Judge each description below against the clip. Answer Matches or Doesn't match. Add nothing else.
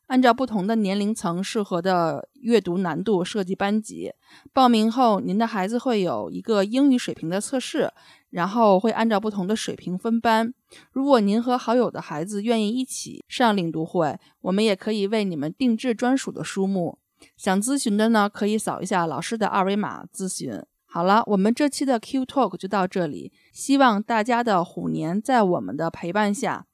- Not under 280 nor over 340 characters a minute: Matches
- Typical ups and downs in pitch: Matches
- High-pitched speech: Matches